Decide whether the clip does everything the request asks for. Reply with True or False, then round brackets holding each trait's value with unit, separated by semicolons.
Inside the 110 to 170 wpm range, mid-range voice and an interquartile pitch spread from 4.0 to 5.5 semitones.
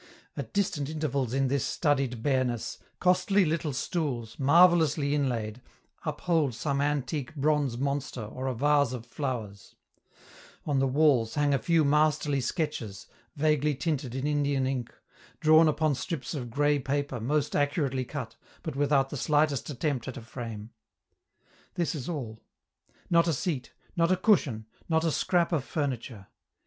False (150 wpm; 145 Hz; 3.3 semitones)